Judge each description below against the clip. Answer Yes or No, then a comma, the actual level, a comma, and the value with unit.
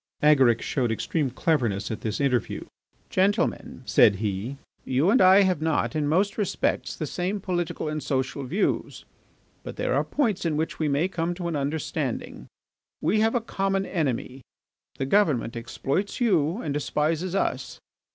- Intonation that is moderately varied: No, wide, 5.9 semitones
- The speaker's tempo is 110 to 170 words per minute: Yes, average, 160 wpm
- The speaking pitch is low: No, medium, 155 Hz